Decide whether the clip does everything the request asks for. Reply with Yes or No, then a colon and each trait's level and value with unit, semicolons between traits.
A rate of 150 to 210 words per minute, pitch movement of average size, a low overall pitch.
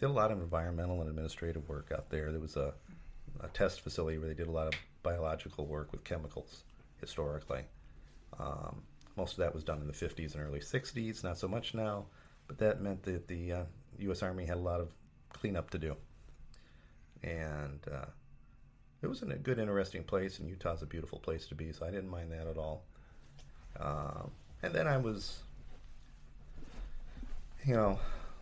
Yes: average, 185 wpm; average, 3.8 semitones; very low, 80 Hz